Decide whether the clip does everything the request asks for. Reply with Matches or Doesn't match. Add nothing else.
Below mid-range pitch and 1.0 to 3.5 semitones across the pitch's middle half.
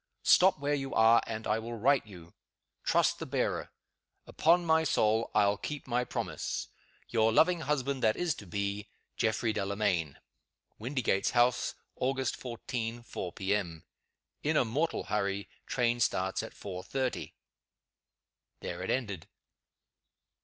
Doesn't match